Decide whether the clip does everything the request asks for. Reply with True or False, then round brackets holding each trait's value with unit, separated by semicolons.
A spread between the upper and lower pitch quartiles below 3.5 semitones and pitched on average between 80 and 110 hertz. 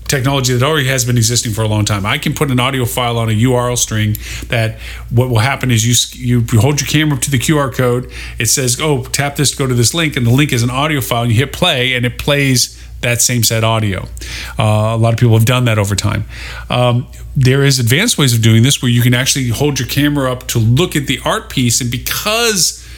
False (3.1 semitones; 125 Hz)